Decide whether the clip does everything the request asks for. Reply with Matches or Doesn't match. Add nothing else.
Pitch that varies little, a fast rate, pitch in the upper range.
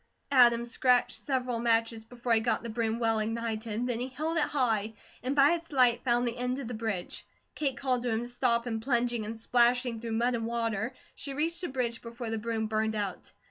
Matches